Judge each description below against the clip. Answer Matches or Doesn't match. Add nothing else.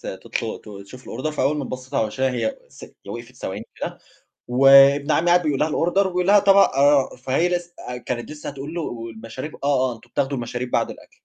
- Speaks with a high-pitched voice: Doesn't match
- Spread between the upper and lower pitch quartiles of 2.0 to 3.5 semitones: Doesn't match